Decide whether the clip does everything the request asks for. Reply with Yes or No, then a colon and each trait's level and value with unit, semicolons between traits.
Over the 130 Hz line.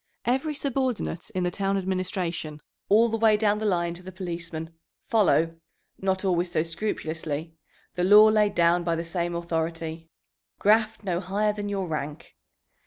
Yes: medium, 185 Hz